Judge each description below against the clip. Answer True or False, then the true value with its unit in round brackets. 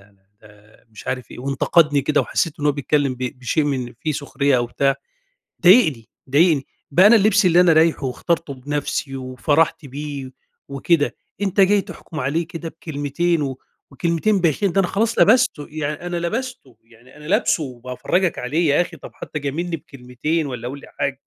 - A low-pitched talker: False (150 Hz)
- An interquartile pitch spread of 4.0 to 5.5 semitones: True (4.4 semitones)